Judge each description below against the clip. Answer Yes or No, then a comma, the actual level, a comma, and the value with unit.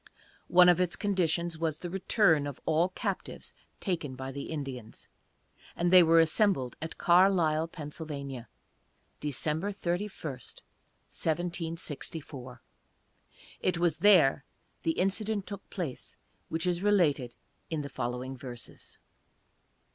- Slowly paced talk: Yes, slow, 115 wpm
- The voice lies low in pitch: No, medium, 165 Hz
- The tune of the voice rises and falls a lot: No, average, 4.1 semitones